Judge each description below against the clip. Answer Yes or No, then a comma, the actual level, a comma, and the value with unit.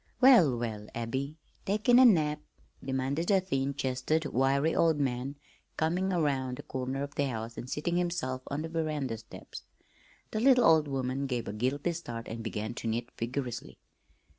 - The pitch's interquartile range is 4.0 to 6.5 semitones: Yes, average, 4.6 semitones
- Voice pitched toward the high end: No, medium, 140 Hz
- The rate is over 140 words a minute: Yes, average, 165 wpm